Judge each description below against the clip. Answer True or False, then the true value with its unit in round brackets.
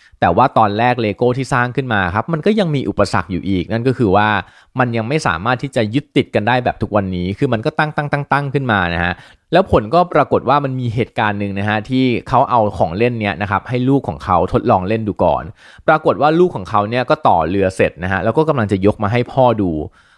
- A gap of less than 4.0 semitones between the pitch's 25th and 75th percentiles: False (4.8 semitones)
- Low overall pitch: True (115 Hz)